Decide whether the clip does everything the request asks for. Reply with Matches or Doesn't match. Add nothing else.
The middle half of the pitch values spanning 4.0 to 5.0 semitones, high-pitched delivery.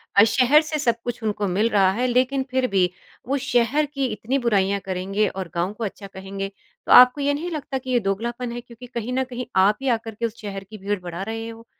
Matches